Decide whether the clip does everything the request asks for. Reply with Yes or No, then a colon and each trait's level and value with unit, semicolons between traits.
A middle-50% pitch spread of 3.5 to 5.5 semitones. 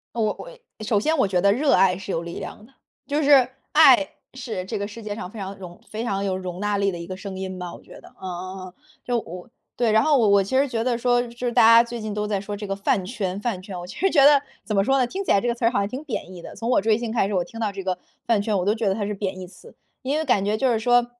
Yes: average, 4.0 semitones